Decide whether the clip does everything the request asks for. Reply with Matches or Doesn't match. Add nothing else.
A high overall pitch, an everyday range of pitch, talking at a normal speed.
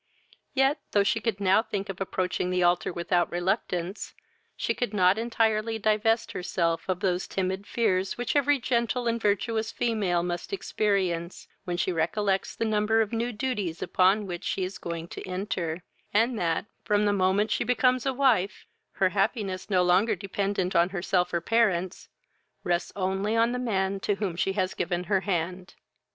Matches